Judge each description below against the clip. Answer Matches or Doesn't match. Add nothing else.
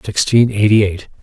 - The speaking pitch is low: Matches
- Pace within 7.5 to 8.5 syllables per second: Doesn't match